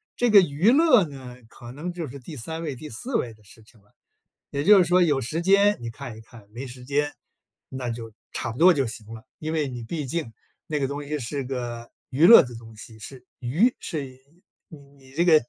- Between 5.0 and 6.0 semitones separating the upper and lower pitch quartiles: Yes, wide, 5.4 semitones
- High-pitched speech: No, medium, 140 Hz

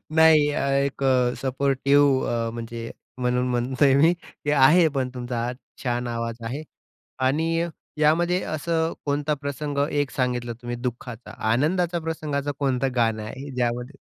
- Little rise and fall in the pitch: No, average, 3.4 semitones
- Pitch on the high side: No, low, 135 Hz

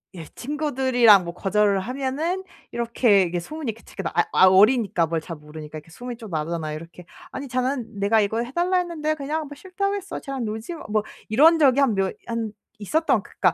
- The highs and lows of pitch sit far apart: Yes, wide, 6.8 semitones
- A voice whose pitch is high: Yes, high, 230 Hz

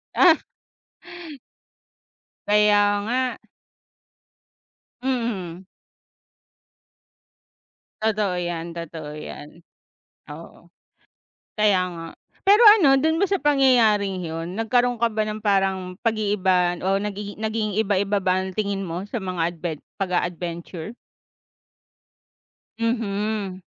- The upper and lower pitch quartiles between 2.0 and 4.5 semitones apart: Yes, average, 3.8 semitones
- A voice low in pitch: No, high, 205 Hz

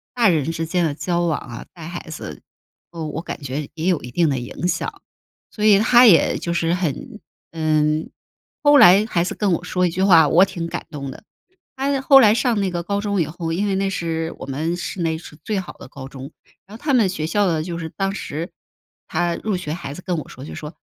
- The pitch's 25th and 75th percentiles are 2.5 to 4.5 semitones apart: Yes, average, 3.8 semitones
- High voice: No, medium, 170 Hz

